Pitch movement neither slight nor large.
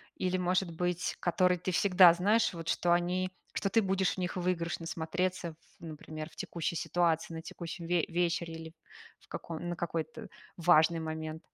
No: narrow, 1.8 semitones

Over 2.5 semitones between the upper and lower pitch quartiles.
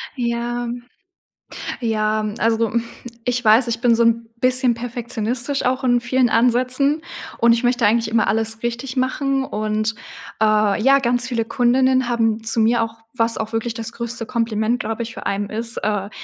No: narrow, 1.8 semitones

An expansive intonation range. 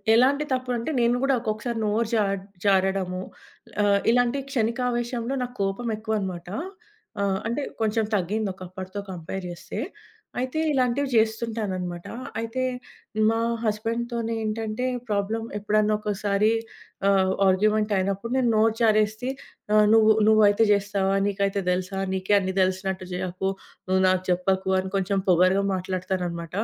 No: average, 3.1 semitones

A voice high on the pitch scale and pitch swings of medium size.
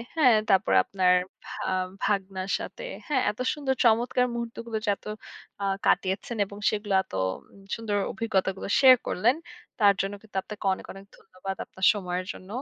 Yes: high, 205 Hz; average, 3.3 semitones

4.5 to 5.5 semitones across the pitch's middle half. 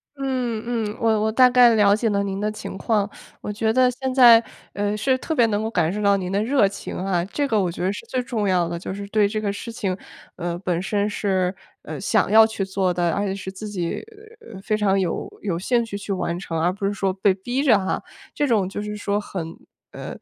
No: average, 2.9 semitones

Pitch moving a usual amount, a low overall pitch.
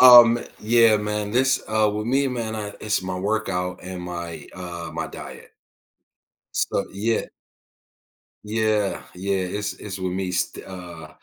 Yes: average, 3.2 semitones; low, 105 Hz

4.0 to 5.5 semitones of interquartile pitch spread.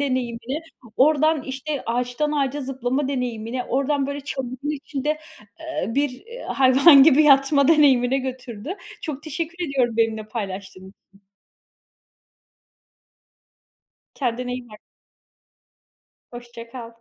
No: average, 3.2 semitones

